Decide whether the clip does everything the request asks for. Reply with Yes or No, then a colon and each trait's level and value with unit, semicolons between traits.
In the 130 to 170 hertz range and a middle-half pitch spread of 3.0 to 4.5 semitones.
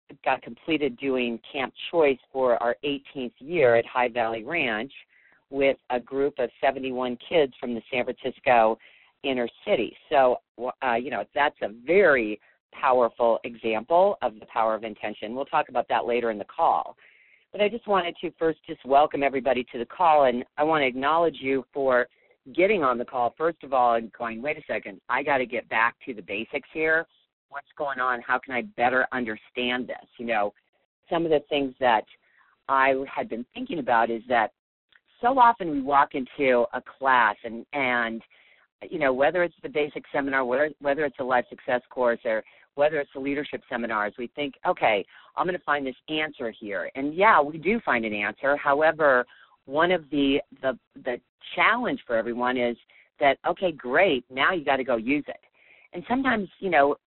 Yes: low, 135 Hz; average, 3.9 semitones